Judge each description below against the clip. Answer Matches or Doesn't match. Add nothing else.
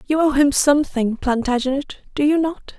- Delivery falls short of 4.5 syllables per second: Doesn't match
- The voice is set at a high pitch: Matches